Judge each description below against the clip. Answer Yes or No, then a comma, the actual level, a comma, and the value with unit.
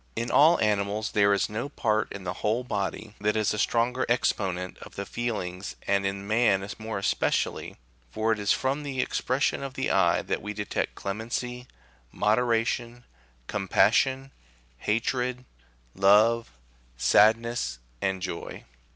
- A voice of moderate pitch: No, low, 110 Hz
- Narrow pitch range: No, average, 3.5 semitones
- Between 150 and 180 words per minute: No, average, 140 wpm